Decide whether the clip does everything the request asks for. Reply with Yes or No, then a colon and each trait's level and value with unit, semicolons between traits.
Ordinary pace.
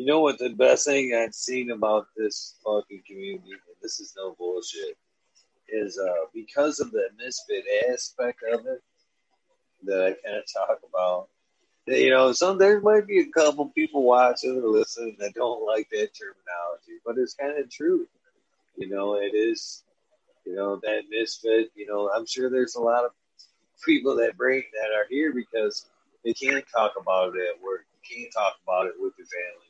Yes: average, 190 wpm